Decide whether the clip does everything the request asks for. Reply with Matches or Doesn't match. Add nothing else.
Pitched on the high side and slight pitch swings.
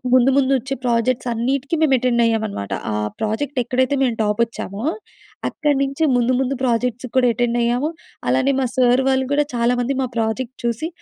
Matches